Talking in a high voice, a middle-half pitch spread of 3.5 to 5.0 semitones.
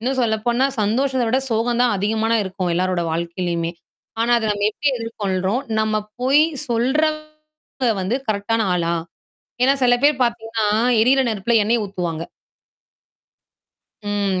Yes: high, 225 Hz; average, 4.1 semitones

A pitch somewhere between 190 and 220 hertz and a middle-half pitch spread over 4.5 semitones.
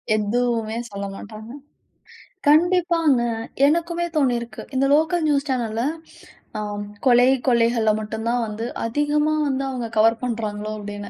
No: high, 240 Hz; average, 5.1 semitones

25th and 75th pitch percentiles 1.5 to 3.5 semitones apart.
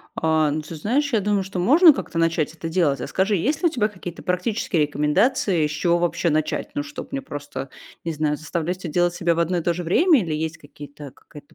No: average, 4.5 semitones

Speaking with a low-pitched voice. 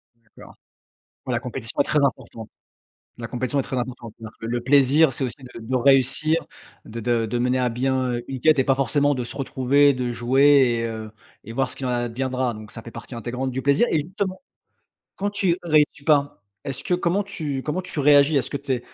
Yes: low, 130 Hz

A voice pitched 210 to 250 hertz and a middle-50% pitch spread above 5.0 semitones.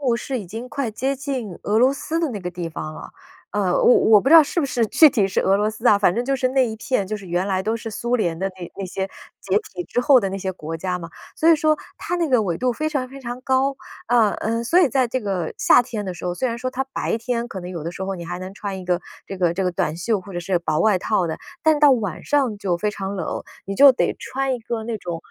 Yes: high, 220 Hz; wide, 5.6 semitones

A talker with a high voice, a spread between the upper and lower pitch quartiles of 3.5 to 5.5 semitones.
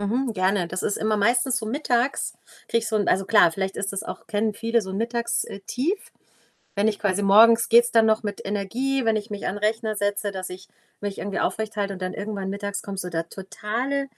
No: high, 210 Hz; average, 2.7 semitones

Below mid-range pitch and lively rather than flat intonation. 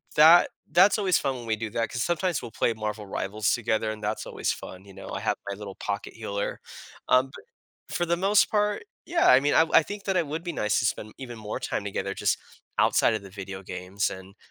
Yes: low, 115 Hz; wide, 8.3 semitones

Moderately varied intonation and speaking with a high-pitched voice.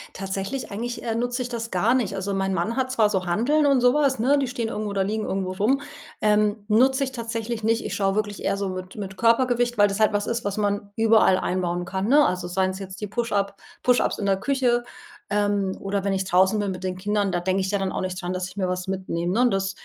Yes: average, 3.5 semitones; high, 205 Hz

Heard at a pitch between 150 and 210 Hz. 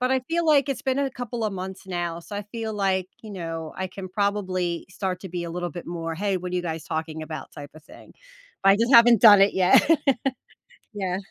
Yes: high, 190 Hz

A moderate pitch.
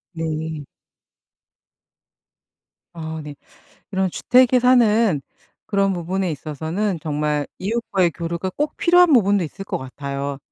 Yes: medium, 180 Hz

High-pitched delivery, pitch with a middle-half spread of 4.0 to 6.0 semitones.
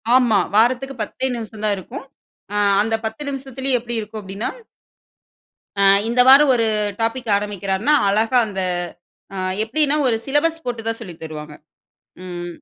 Yes: high, 225 Hz; average, 4.3 semitones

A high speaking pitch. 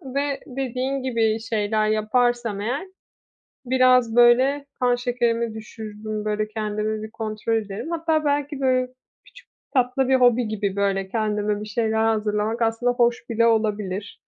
Yes: high, 225 Hz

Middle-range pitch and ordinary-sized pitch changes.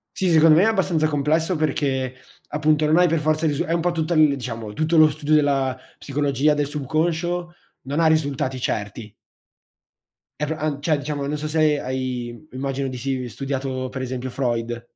Yes: medium, 145 Hz; average, 3.1 semitones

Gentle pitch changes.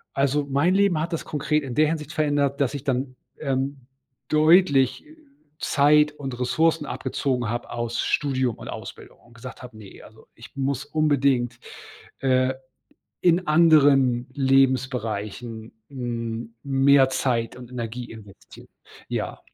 No: average, 3.3 semitones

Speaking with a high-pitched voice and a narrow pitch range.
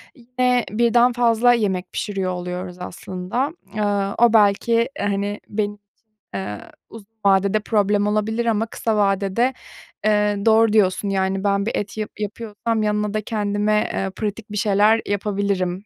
Yes: high, 210 Hz; narrow, 2.1 semitones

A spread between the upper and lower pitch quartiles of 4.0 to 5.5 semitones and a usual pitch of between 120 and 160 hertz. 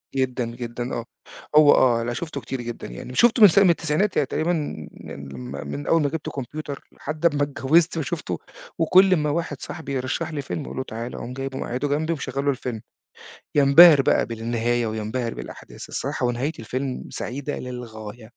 Yes: average, 4.5 semitones; low, 135 Hz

